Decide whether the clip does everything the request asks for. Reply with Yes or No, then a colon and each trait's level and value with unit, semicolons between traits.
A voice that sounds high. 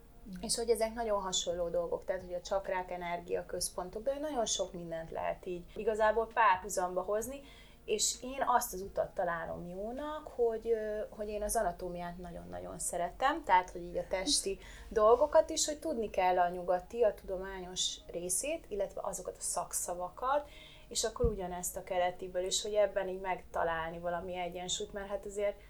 Yes: high, 200 Hz